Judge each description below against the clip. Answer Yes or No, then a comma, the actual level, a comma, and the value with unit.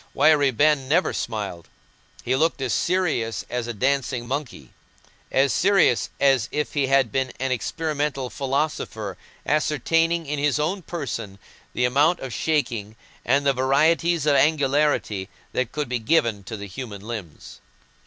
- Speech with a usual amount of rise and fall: Yes, average, 4.2 semitones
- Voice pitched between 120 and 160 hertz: Yes, low, 135 Hz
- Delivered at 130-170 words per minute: Yes, average, 145 wpm